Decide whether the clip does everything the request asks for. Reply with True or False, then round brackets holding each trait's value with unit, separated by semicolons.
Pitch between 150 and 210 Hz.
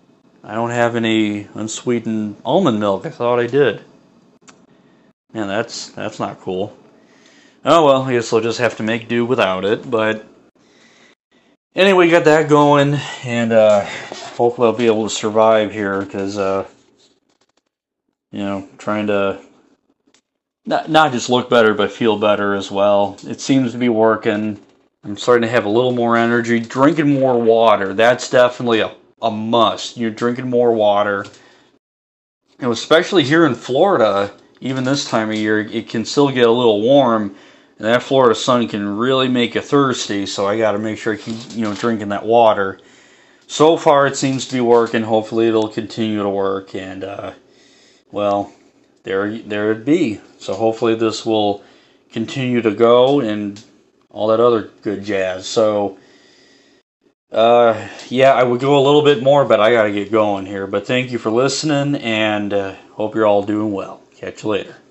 False (110 Hz)